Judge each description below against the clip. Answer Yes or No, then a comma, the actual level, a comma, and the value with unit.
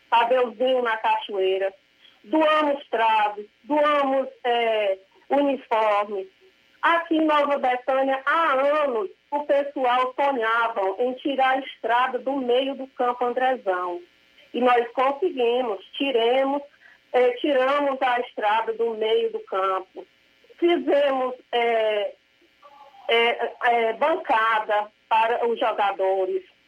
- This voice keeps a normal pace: No, slow, 105 wpm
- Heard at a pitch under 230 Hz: No, very high, 250 Hz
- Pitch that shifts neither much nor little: Yes, average, 4.0 semitones